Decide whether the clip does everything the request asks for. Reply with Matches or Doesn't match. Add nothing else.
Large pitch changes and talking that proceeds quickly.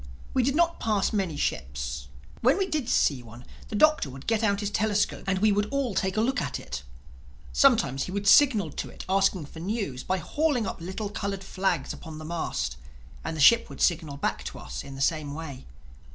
Matches